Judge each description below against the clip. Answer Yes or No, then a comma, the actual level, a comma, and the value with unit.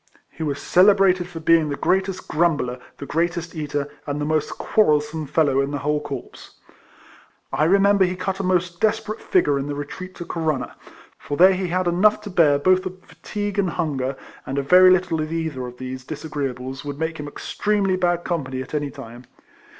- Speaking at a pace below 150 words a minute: No, average, 190 wpm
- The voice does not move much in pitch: No, average, 4.3 semitones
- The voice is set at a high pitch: No, medium, 160 Hz